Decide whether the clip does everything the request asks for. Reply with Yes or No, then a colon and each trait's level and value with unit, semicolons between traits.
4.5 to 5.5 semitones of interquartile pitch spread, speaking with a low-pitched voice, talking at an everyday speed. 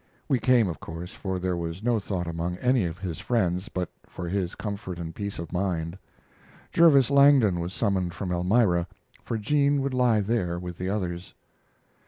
Yes: average, 4.9 semitones; very low, 95 Hz; average, 180 wpm